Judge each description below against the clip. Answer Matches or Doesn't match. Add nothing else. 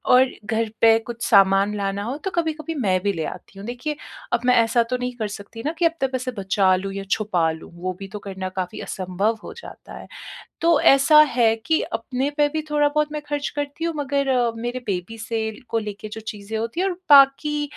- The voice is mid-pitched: Doesn't match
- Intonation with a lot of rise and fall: Matches